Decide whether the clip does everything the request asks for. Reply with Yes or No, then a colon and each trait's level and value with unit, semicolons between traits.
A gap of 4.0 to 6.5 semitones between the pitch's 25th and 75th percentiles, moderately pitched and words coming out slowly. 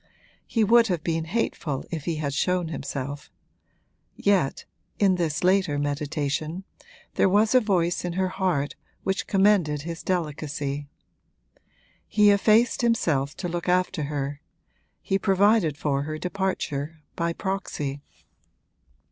Yes: average, 4.7 semitones; medium, 170 Hz; slow, 125 wpm